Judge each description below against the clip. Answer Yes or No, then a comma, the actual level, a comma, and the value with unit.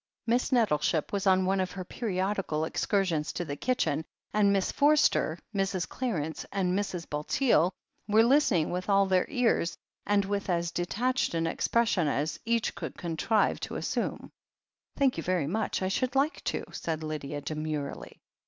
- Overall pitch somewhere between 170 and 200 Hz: Yes, high, 190 Hz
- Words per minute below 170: Yes, average, 160 wpm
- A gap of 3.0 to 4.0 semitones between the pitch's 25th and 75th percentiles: No, average, 5.1 semitones